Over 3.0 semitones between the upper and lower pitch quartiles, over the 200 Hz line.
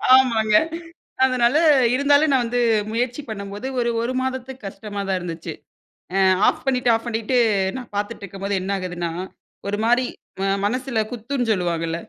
Yes: average, 4.2 semitones; high, 230 Hz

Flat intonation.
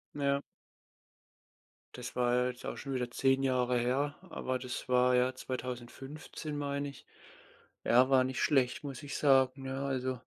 Yes: narrow, 1.8 semitones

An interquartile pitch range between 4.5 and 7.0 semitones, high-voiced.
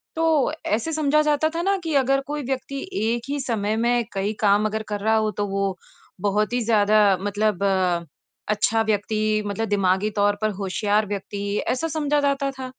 Yes: average, 5.0 semitones; high, 220 Hz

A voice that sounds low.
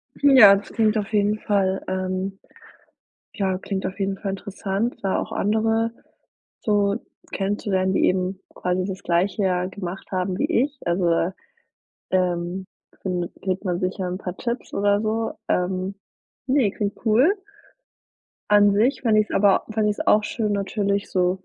No: high, 195 Hz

